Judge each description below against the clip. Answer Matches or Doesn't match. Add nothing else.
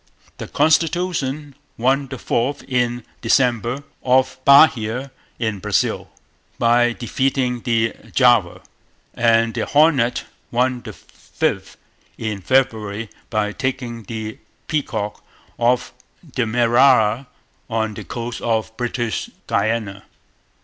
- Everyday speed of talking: Doesn't match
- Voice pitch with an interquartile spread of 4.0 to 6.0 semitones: Doesn't match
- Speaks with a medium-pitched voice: Doesn't match